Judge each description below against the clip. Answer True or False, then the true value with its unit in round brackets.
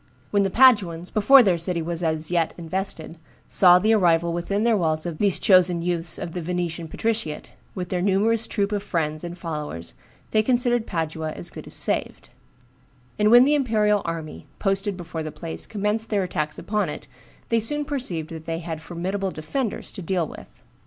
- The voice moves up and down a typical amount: True (4.2 semitones)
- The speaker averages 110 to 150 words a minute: False (185 wpm)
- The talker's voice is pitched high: False (180 Hz)